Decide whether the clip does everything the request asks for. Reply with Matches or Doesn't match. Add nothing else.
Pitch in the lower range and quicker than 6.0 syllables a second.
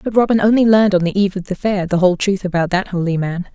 Doesn't match